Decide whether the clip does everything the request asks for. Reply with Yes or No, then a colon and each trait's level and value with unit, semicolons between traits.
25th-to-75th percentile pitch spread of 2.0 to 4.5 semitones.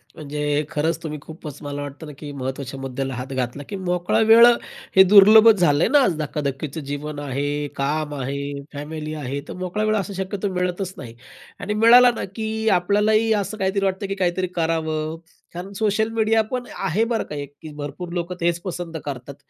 No: wide, 5.5 semitones